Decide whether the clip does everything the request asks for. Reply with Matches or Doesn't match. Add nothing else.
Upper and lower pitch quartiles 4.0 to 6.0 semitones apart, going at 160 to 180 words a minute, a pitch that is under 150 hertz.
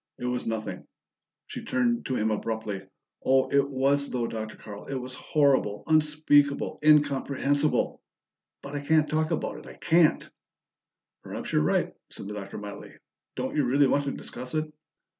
Matches